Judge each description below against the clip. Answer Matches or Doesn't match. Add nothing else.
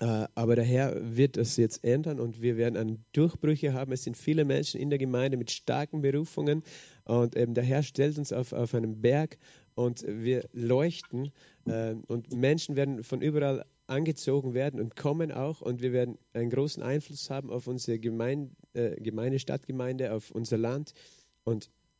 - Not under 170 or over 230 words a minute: Matches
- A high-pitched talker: Doesn't match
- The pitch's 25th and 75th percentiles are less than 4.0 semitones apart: Matches